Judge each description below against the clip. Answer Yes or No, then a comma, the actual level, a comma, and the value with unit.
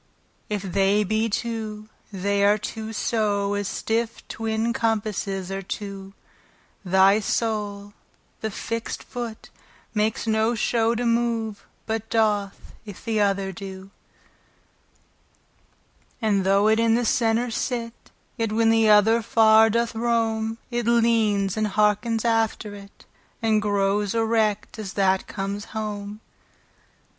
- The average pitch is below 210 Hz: No, high, 215 Hz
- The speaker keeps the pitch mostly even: Yes, narrow, 1.9 semitones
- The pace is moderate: No, slow, 125 wpm